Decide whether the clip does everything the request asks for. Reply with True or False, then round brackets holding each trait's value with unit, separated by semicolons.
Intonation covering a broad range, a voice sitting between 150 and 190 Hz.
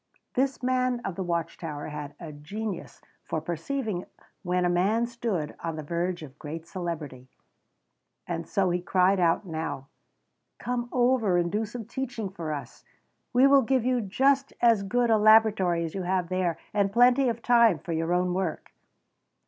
True (5.8 semitones; 185 Hz)